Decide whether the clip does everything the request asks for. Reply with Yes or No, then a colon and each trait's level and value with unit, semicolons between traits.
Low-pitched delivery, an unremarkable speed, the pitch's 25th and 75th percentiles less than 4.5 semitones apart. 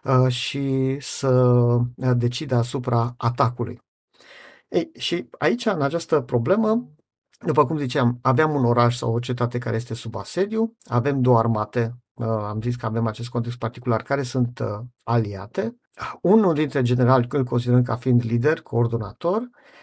Yes: low, 125 Hz; average, 140 wpm; average, 3.3 semitones